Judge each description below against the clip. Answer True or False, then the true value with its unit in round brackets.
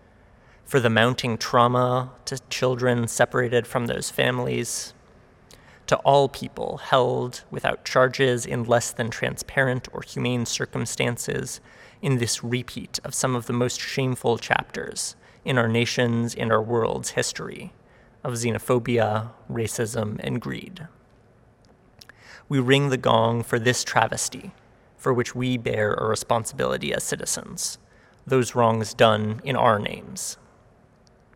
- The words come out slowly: True (125 wpm)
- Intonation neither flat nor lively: False (1.7 semitones)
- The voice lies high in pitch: False (120 Hz)